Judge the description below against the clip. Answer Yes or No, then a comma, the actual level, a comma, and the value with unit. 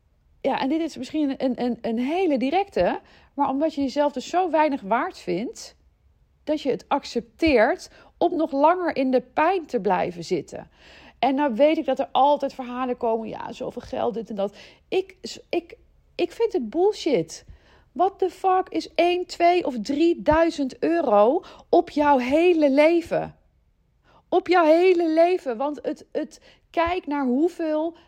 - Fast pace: No, average, 160 wpm